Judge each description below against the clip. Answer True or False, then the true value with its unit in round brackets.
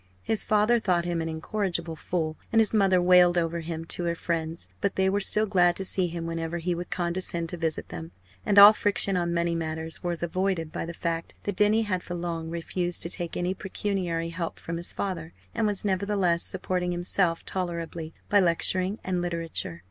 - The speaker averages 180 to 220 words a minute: True (200 wpm)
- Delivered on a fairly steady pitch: True (2.3 semitones)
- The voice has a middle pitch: True (175 Hz)